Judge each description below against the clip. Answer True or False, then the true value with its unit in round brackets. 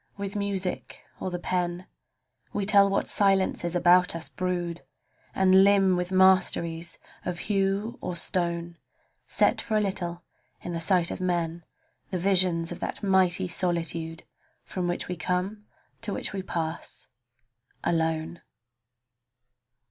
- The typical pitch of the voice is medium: True (180 Hz)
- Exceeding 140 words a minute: False (135 wpm)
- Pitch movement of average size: False (2.0 semitones)